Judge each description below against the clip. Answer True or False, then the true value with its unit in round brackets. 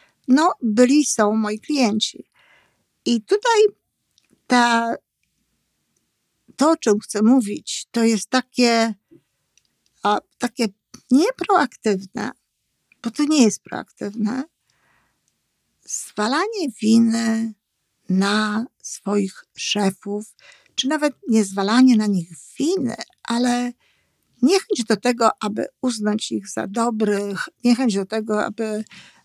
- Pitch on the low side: False (230 Hz)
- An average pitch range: True (3.4 semitones)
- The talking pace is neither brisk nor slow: False (100 wpm)